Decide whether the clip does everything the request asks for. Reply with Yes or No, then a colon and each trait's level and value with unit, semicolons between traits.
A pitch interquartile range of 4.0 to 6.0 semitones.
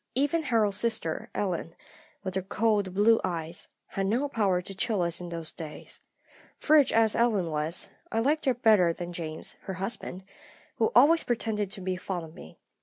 Yes: average, 4.5 semitones